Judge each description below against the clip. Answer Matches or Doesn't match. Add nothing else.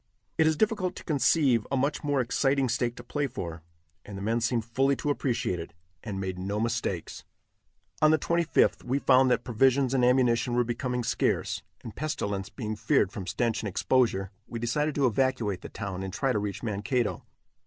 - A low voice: Matches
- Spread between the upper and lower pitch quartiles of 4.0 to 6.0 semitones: Matches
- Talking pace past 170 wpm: Matches